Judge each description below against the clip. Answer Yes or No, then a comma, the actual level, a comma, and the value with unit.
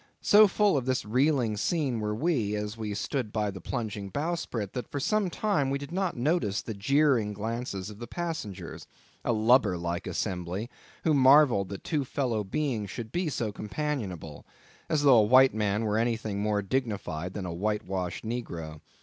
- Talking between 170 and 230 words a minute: Yes, average, 175 wpm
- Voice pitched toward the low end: Yes, low, 110 Hz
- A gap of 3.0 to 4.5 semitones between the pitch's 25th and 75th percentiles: No, wide, 5.4 semitones